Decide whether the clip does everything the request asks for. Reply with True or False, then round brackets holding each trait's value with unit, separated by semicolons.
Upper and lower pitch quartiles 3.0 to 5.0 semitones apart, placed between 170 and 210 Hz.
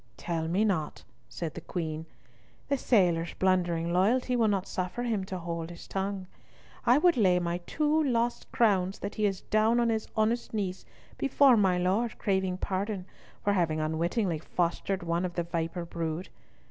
True (4.2 semitones; 190 Hz)